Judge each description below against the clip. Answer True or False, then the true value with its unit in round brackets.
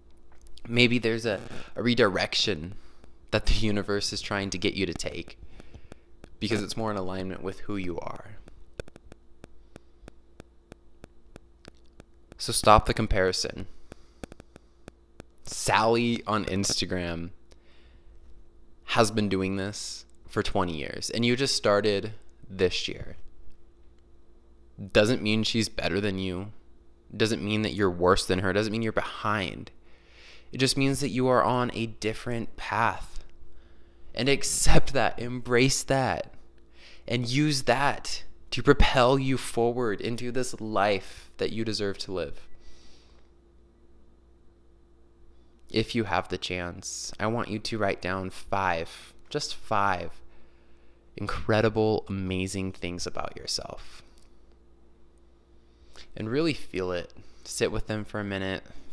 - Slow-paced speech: True (120 wpm)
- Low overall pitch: True (95 Hz)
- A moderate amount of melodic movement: True (4.5 semitones)